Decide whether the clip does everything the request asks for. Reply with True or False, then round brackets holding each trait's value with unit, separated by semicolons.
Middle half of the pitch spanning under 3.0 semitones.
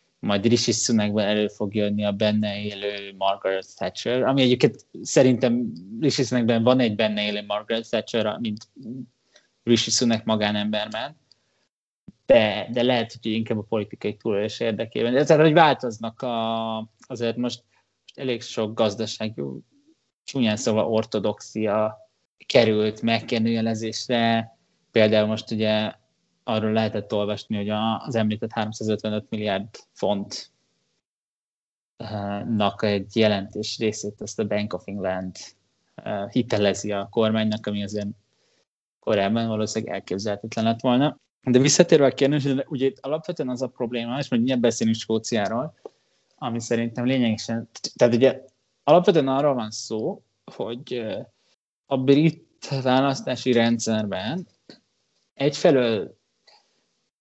True (2.5 semitones)